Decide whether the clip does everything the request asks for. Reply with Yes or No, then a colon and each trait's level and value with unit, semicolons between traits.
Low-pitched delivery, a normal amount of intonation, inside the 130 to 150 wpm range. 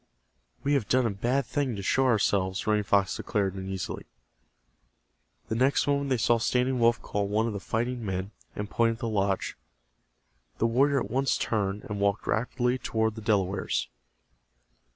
No: low, 110 Hz; average, 3.8 semitones; average, 170 wpm